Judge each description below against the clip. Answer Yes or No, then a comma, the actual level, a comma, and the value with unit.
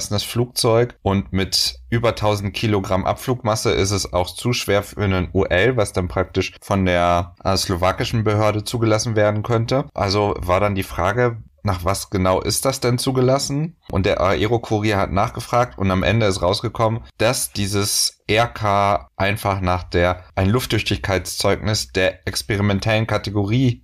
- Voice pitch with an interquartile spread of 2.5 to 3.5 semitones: Yes, average, 3.1 semitones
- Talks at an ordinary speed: Yes, average, 150 wpm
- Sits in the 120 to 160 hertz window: No, low, 100 Hz